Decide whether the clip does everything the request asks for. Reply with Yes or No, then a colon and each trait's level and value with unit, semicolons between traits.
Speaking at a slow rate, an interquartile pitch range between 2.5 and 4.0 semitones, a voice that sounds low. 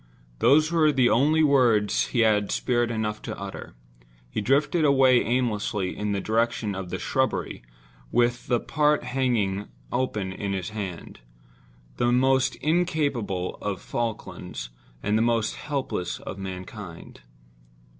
No: slow, 130 wpm; average, 4.9 semitones; low, 115 Hz